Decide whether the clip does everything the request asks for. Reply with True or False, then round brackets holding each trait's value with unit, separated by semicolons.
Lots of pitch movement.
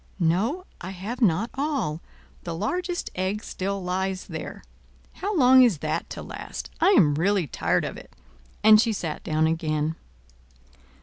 True (6.4 semitones)